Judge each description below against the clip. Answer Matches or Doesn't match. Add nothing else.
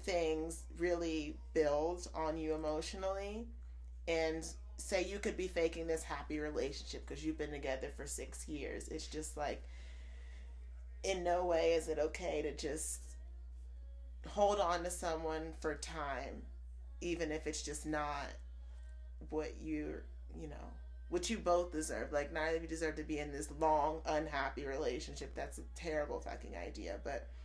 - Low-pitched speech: Doesn't match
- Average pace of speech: Matches